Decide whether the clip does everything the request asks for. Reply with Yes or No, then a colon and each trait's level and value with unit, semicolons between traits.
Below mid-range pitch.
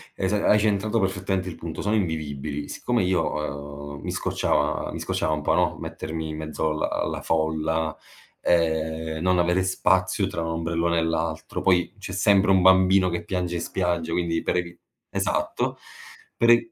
Yes: very low, 85 Hz